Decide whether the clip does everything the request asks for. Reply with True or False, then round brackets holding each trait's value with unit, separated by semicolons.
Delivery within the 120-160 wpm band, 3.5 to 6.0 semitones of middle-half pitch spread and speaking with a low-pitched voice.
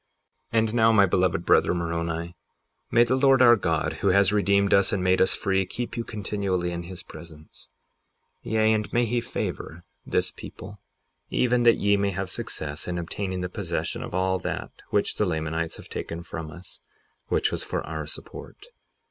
False (180 wpm; 4.0 semitones; 95 Hz)